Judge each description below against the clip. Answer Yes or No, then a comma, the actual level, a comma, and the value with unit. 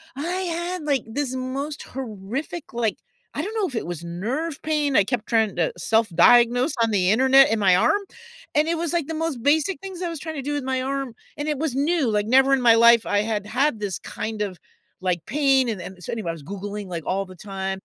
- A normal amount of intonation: No, wide, 6.2 semitones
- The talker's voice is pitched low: No, high, 245 Hz